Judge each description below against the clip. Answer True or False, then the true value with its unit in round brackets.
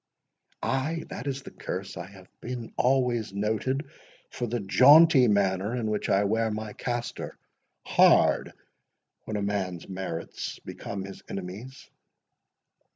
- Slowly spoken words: True (125 wpm)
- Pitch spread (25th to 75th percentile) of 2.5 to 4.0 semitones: False (4.4 semitones)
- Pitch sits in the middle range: False (110 Hz)